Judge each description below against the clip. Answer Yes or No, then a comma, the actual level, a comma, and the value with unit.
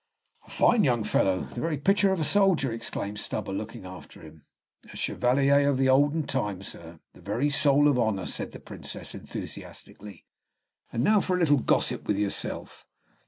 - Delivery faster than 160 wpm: Yes, average, 175 wpm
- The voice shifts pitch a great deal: Yes, wide, 6.0 semitones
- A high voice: No, low, 130 Hz